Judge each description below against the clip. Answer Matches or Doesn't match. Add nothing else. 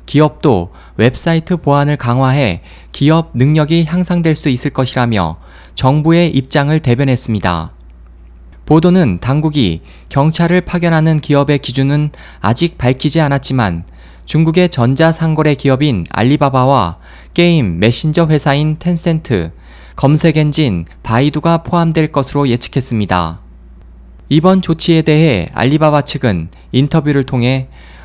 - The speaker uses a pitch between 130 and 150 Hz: Matches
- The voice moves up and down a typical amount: Doesn't match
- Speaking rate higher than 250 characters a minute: Matches